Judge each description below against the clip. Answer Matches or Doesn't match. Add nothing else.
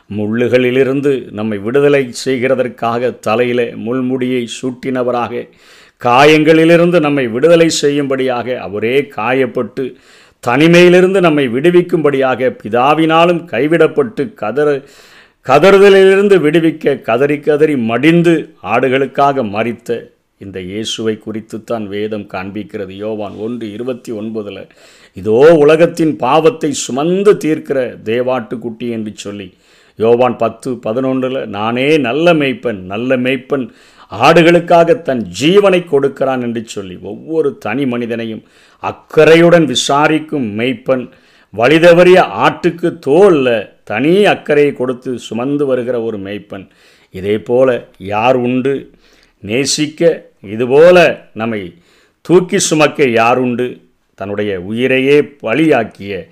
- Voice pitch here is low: Matches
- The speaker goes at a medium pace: Matches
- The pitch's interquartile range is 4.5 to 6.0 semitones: Matches